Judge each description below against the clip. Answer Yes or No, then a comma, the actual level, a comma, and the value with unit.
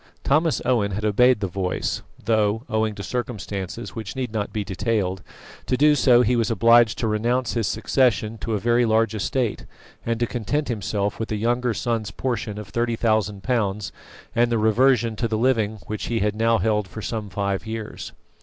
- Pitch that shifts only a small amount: Yes, narrow, 2.3 semitones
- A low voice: Yes, low, 110 Hz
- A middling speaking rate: Yes, average, 190 wpm